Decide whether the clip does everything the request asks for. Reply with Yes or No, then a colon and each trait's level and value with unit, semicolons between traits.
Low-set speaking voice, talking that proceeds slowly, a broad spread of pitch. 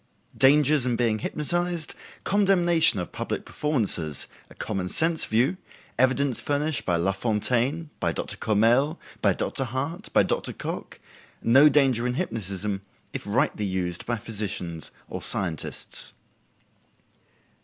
Yes: low, 125 Hz; slow, 100 wpm; wide, 6.5 semitones